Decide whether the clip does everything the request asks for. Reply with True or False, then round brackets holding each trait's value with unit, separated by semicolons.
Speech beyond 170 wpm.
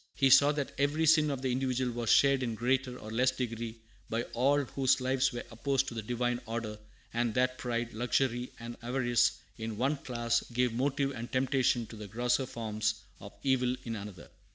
True (190 wpm)